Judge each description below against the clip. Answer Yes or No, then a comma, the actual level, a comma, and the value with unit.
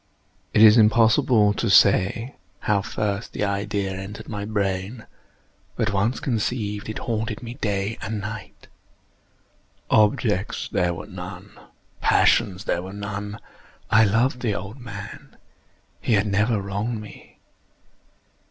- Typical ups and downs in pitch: No, narrow, 2.0 semitones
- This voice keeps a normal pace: No, slow, 125 wpm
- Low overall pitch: Yes, low, 105 Hz